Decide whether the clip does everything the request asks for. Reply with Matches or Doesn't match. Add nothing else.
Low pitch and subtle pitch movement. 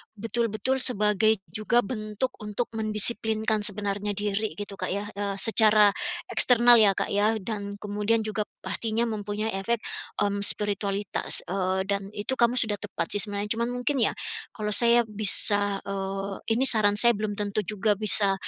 Doesn't match